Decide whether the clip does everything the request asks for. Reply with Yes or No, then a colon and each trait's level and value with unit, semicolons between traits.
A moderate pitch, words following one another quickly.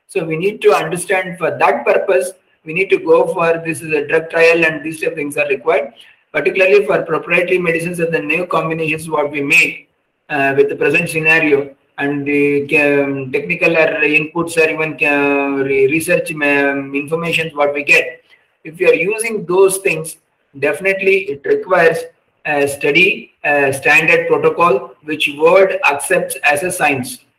No: medium, 160 Hz; average, 160 wpm